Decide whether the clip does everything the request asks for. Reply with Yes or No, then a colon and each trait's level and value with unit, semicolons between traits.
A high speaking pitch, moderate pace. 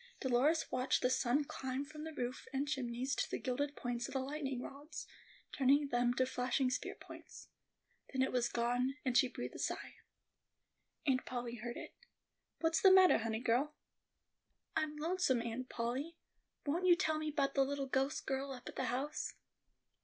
Yes: very high, 265 Hz; average, 175 wpm